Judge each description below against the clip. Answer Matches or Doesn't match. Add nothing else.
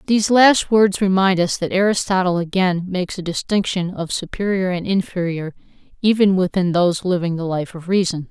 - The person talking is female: Matches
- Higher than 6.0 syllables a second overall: Doesn't match